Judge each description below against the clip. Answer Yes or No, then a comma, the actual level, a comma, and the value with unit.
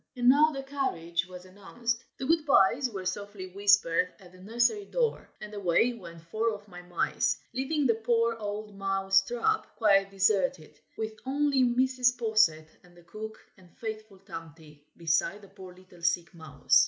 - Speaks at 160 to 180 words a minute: Yes, average, 165 wpm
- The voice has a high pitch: Yes, high, 205 Hz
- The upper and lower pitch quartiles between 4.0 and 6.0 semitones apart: Yes, average, 4.9 semitones